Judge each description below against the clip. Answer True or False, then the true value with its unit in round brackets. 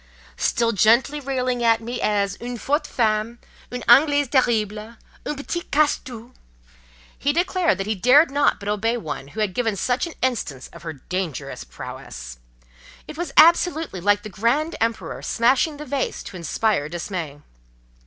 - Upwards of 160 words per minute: False (150 wpm)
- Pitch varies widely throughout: True (6.2 semitones)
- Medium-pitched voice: False (230 Hz)